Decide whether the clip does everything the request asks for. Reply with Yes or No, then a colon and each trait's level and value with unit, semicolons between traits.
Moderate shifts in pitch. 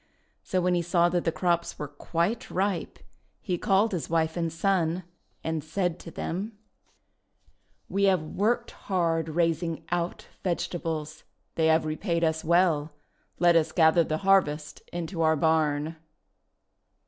No: narrow, 2.2 semitones